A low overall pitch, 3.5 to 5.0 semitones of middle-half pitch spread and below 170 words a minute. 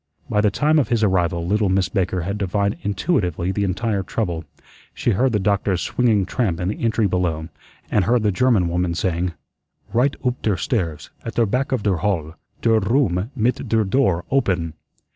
No: low, 100 Hz; average, 4.1 semitones; average, 185 wpm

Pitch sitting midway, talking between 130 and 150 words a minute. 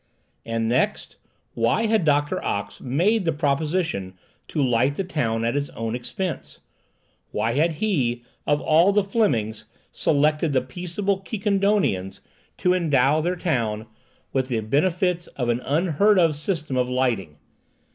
Yes: medium, 145 Hz; average, 140 wpm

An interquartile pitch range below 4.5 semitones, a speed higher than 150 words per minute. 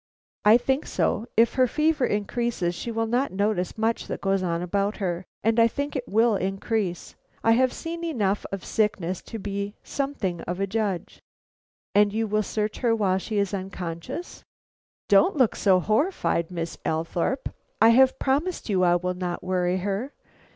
Yes: average, 4.1 semitones; average, 170 wpm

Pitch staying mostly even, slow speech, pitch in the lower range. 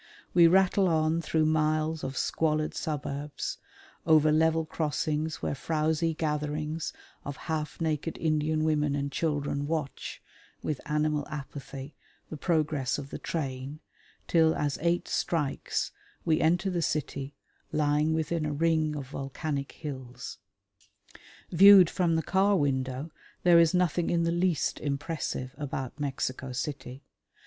No: narrow, 2.3 semitones; slow, 130 wpm; medium, 155 Hz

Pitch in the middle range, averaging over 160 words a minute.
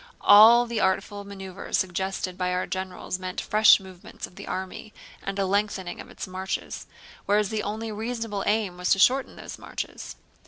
No: high, 195 Hz; average, 170 wpm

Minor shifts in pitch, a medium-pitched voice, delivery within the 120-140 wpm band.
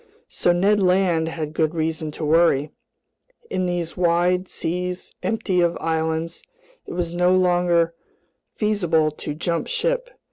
Yes: narrow, 2.0 semitones; medium, 175 Hz; slow, 135 wpm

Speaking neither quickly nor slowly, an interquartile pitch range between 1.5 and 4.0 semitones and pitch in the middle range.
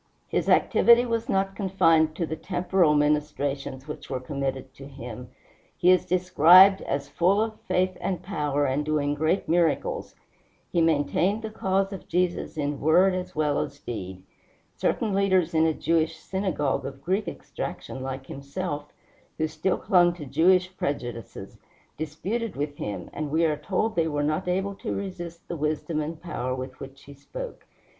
No: average, 165 wpm; average, 4.4 semitones; medium, 160 Hz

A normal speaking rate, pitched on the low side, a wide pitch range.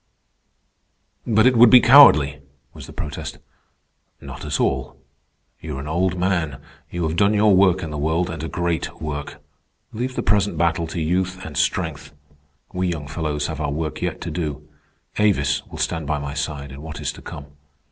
No: average, 190 wpm; very low, 80 Hz; average, 4.0 semitones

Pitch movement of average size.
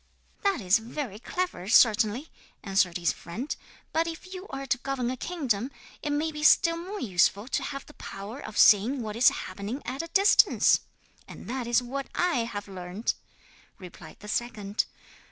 No: wide, 6.5 semitones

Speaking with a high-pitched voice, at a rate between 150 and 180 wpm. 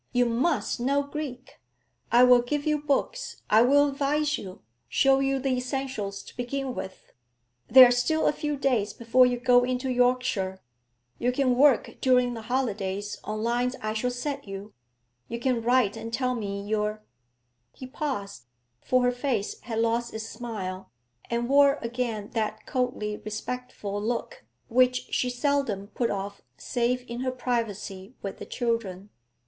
Yes: high, 245 Hz; average, 160 wpm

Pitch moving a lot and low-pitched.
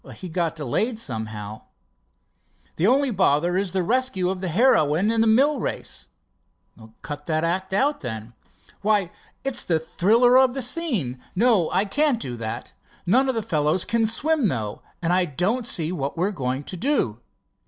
No: wide, 7.6 semitones; medium, 185 Hz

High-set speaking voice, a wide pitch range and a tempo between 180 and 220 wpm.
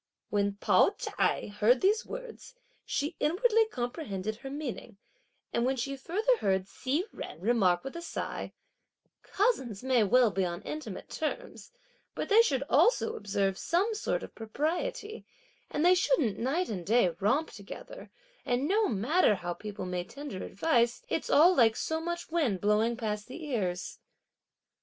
No: very high, 255 Hz; wide, 8.6 semitones; average, 155 wpm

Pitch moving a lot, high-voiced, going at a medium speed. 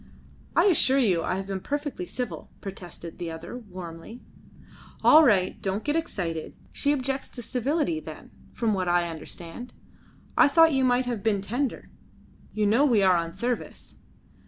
Yes: wide, 6.6 semitones; high, 220 Hz; average, 160 wpm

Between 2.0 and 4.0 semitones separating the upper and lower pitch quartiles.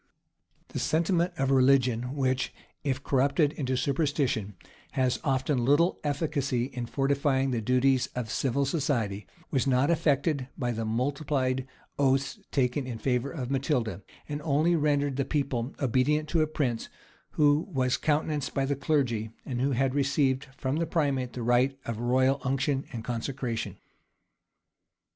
Yes: narrow, 2.4 semitones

